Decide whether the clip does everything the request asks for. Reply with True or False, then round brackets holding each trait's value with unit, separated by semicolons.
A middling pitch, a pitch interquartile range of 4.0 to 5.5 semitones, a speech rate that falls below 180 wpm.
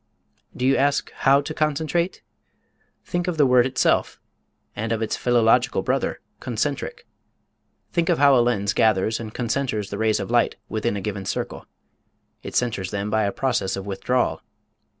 False (120 Hz; 4.4 semitones; 165 wpm)